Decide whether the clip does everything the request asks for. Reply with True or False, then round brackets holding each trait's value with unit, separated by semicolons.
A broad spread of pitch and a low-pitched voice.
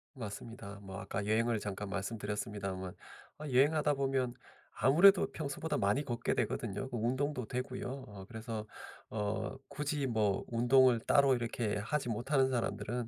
False (4.4 semitones; 120 Hz)